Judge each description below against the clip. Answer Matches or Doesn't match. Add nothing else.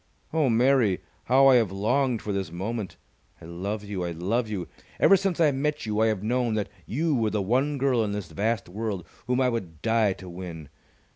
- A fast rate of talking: Matches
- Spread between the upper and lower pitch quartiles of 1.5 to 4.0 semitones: Doesn't match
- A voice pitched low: Matches